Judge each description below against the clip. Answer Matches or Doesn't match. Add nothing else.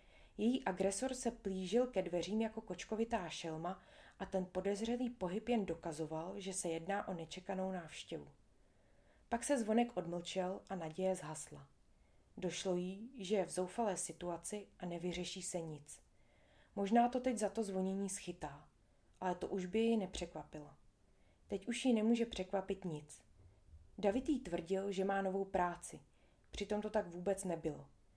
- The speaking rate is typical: Matches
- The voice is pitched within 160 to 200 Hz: Matches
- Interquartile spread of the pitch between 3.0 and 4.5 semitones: Matches